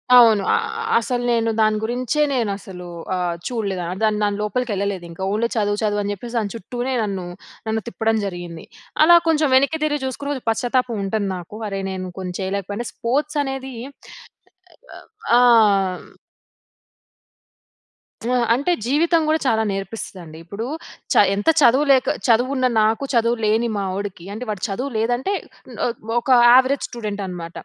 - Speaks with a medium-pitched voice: No, high, 225 Hz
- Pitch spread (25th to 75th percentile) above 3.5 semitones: Yes, average, 4.1 semitones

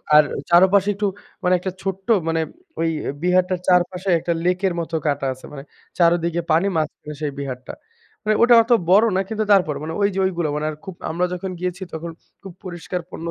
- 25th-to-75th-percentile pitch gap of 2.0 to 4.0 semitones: Yes, average, 2.8 semitones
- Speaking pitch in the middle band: Yes, medium, 180 Hz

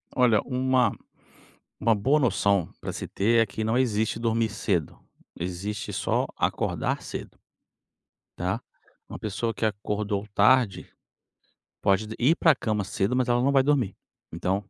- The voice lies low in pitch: Yes, low, 110 Hz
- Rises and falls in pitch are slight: No, average, 3.8 semitones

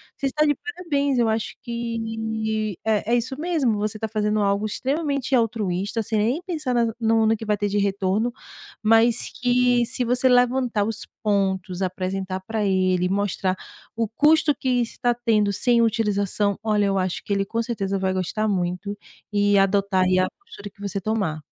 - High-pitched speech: Yes, high, 215 Hz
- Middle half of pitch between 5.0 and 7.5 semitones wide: No, average, 3.3 semitones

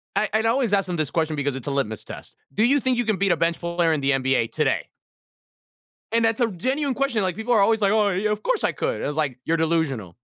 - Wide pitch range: Yes, wide, 6.7 semitones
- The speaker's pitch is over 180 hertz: Yes, high, 190 Hz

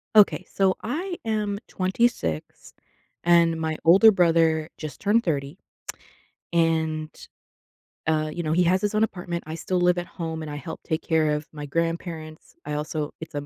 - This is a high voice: No, medium, 165 Hz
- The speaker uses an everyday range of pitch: Yes, average, 3.0 semitones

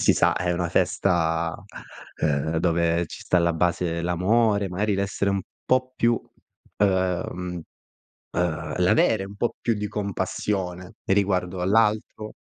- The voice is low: Yes, very low, 90 Hz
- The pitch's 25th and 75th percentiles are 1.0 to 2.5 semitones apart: No, average, 2.9 semitones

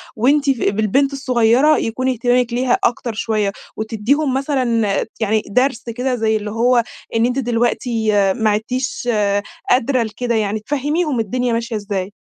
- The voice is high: Yes, high, 240 Hz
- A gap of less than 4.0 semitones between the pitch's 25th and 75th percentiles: Yes, average, 2.9 semitones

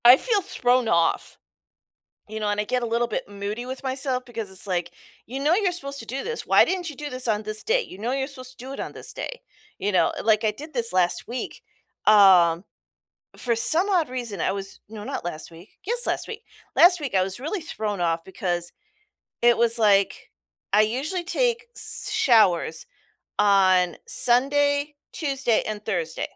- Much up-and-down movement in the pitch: Yes, wide, 5.8 semitones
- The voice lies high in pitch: Yes, high, 235 Hz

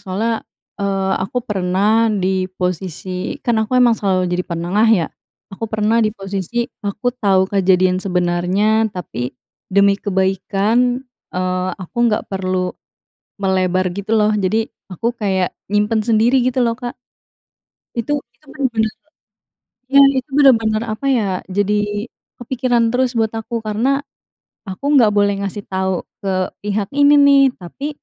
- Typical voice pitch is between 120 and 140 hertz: No, high, 205 Hz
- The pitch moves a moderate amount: Yes, average, 3.5 semitones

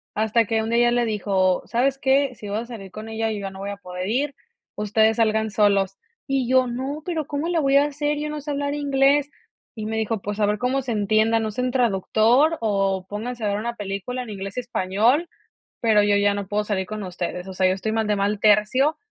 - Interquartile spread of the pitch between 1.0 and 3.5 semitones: No, average, 4.2 semitones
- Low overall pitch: No, high, 220 Hz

